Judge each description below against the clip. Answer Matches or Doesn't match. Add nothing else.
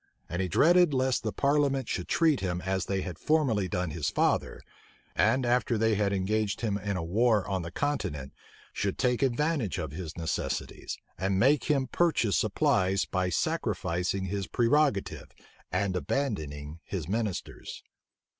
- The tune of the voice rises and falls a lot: Matches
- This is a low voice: Matches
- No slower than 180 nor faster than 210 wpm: Doesn't match